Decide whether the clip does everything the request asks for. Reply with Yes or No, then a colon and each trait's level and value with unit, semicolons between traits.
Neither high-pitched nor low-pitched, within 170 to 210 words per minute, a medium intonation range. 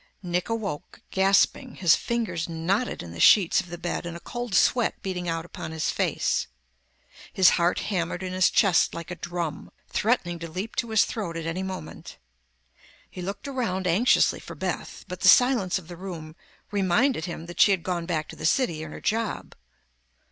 Yes: medium, 180 Hz; average, 190 wpm; average, 3.5 semitones